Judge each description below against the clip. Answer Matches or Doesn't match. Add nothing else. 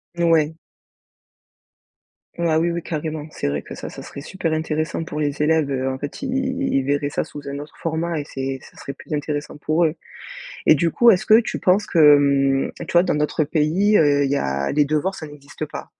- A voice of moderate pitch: Matches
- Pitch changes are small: Doesn't match